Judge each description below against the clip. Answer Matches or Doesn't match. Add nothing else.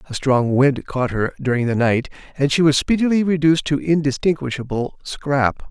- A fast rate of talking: Doesn't match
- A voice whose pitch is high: Doesn't match